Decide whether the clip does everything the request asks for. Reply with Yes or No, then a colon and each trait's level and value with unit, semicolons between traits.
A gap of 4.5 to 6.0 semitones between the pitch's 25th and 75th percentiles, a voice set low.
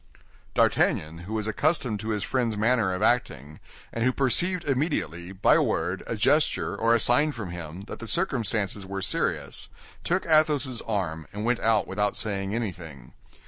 Yes: average, 5.1 semitones; low, 110 Hz